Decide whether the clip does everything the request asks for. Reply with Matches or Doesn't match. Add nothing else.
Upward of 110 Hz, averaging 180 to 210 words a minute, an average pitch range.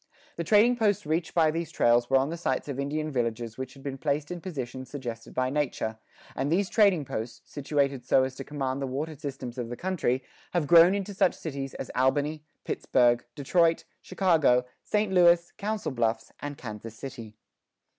Matches